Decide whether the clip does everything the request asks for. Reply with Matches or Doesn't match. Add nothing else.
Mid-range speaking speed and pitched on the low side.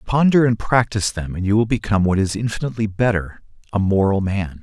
Matches